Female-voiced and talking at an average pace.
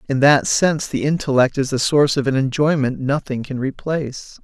No: male; average, 190 wpm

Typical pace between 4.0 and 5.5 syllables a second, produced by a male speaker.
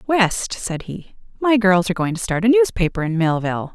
No: 5.3 syllables/s; female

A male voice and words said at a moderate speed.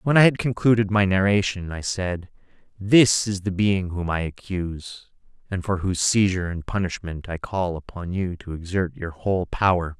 Yes: male; average, 180 wpm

